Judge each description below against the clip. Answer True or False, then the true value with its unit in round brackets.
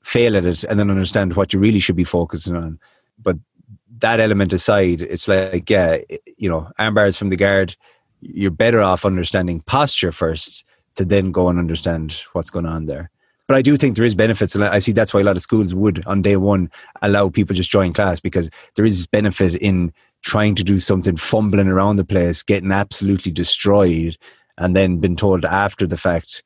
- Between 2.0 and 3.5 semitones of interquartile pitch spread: True (2.6 semitones)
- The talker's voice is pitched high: False (95 Hz)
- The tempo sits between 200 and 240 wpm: True (205 wpm)